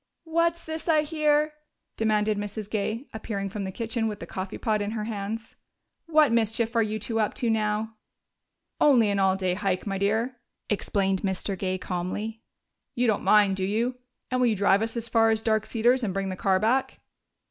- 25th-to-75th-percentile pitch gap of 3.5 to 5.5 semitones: No, average, 2.7 semitones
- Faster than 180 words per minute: Yes, average, 195 wpm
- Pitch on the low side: No, high, 220 Hz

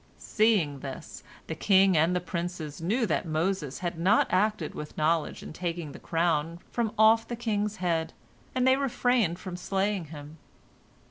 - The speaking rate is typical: Yes, average, 160 wpm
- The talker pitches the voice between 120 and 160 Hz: No, medium, 175 Hz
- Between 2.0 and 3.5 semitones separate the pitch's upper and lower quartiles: No, average, 4.6 semitones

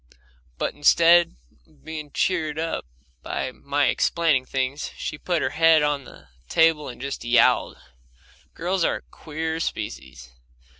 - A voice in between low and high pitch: Yes, medium, 150 Hz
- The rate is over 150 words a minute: No, average, 140 wpm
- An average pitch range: Yes, average, 3.3 semitones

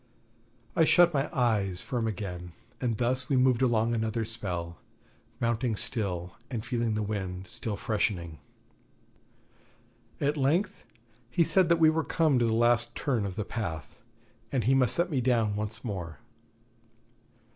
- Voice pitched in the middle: No, low, 115 Hz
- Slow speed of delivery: No, average, 150 wpm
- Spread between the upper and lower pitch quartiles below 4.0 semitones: No, average, 4.3 semitones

